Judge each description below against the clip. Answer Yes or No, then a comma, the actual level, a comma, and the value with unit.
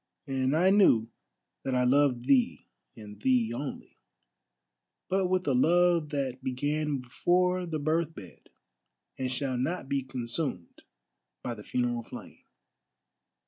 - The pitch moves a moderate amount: Yes, average, 4.3 semitones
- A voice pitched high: No, low, 135 Hz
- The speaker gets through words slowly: Yes, slow, 130 wpm